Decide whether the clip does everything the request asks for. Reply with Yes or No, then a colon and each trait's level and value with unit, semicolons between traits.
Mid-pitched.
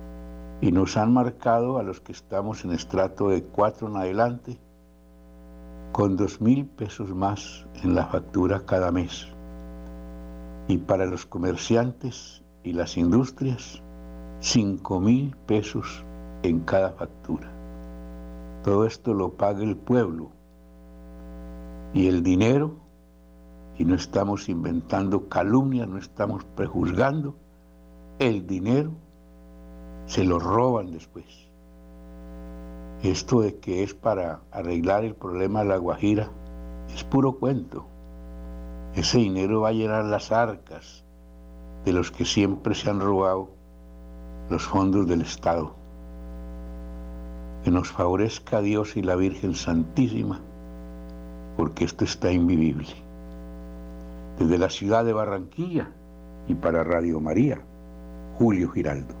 No: very low, 85 Hz